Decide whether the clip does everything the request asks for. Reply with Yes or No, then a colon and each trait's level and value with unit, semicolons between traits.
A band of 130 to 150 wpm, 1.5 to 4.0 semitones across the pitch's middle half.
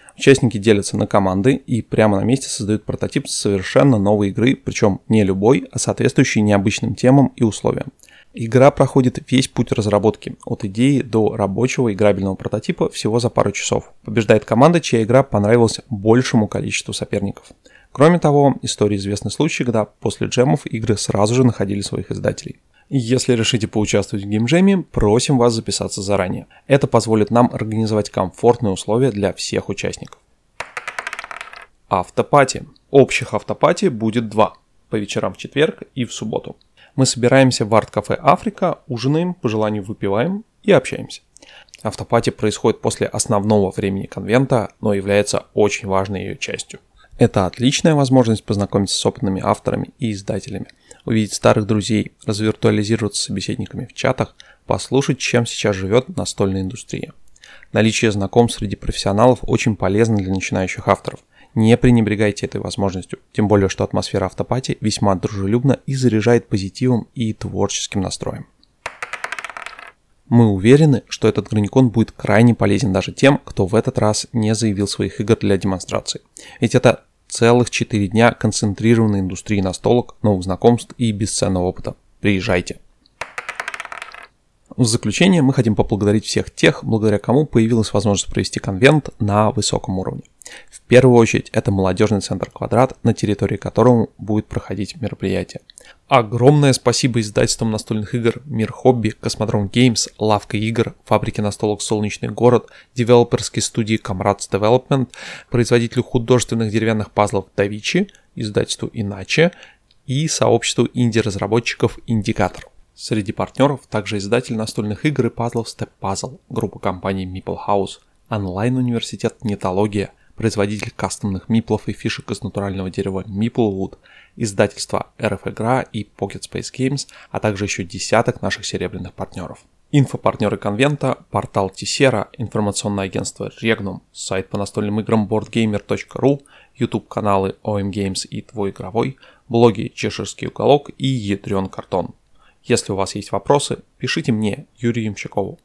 Yes: average, 135 wpm; average, 3.1 semitones